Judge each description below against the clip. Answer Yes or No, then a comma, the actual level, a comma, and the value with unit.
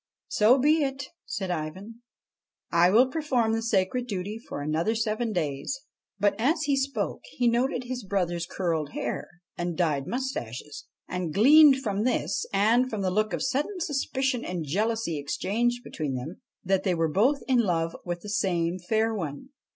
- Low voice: No, high, 210 Hz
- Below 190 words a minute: Yes, average, 175 wpm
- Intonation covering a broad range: Yes, wide, 6.4 semitones